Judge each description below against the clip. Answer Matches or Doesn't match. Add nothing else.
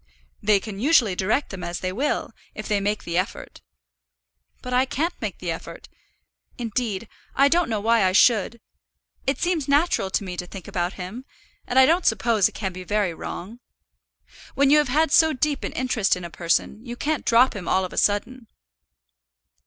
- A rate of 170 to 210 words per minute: Matches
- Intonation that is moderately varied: Doesn't match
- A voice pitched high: Matches